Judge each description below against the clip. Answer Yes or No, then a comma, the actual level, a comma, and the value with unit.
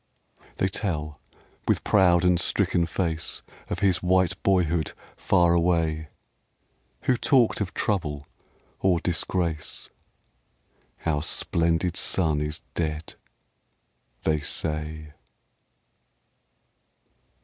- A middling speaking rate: No, slow, 95 wpm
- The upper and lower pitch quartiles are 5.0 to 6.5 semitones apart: No, average, 2.7 semitones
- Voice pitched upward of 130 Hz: No, very low, 85 Hz